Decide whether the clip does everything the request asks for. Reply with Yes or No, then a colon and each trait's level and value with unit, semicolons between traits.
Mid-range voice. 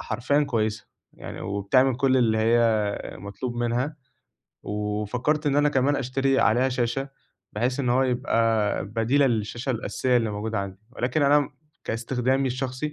No: low, 125 Hz